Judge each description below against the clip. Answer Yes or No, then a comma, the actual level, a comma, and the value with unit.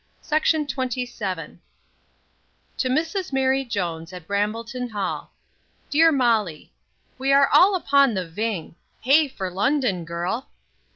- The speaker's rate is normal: No, slow, 125 wpm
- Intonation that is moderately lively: No, wide, 6.5 semitones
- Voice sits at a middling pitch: No, high, 240 Hz